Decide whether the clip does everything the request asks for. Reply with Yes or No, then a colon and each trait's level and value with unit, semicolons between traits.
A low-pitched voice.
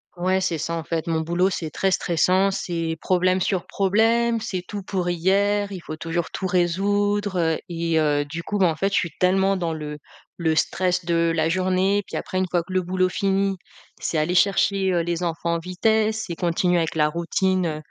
No: medium, 180 Hz